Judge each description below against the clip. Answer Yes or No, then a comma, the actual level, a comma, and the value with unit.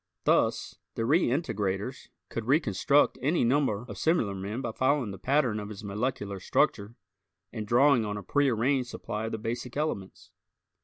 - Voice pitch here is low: Yes, low, 115 Hz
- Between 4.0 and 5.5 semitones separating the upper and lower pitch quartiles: Yes, average, 4.7 semitones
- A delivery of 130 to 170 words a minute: Yes, average, 155 wpm